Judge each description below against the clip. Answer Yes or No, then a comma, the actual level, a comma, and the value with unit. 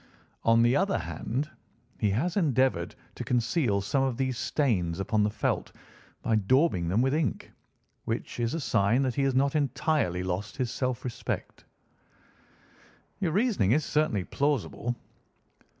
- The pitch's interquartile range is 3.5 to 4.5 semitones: No, average, 5.1 semitones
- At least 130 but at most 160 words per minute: Yes, average, 150 wpm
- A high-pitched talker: No, low, 125 Hz